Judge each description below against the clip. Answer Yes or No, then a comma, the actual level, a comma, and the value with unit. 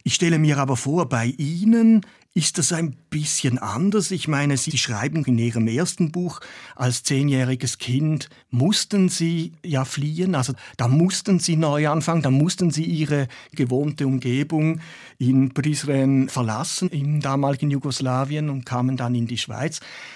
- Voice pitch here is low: No, medium, 145 Hz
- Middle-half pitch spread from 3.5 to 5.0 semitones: Yes, average, 4.0 semitones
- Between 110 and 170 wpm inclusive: Yes, average, 150 wpm